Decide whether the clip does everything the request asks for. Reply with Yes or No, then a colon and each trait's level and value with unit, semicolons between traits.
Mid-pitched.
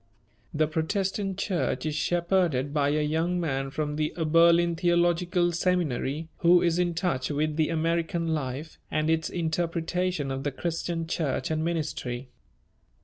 Yes: medium, 165 Hz